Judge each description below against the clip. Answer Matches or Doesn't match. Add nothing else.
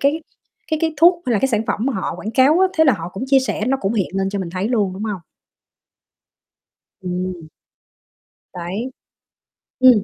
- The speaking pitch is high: Matches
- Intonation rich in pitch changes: Matches